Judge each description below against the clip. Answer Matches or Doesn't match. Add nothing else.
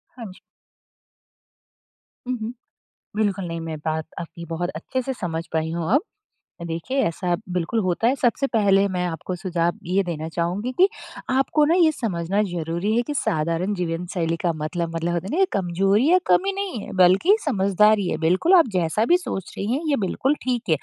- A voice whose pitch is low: Doesn't match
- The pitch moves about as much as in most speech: Doesn't match